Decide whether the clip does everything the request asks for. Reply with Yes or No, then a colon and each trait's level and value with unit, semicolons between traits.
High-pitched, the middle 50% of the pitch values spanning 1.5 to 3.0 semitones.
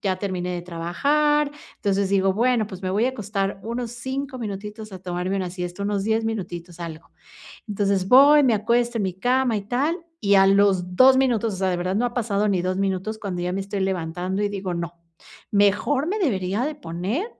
No: high, 200 Hz; average, 4.4 semitones